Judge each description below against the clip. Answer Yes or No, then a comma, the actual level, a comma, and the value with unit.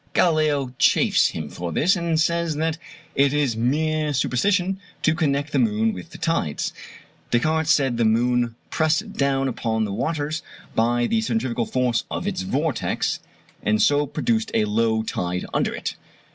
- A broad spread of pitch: Yes, wide, 5.7 semitones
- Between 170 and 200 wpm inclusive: No, average, 160 wpm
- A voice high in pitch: No, medium, 145 Hz